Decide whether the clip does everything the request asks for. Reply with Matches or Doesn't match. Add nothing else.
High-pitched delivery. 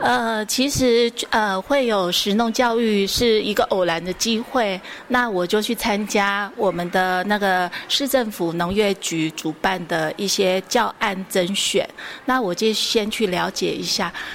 Matches